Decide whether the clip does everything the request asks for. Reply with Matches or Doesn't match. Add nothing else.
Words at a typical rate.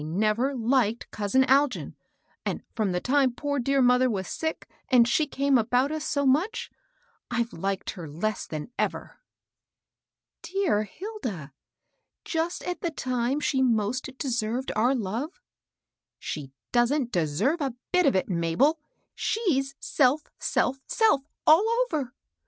Matches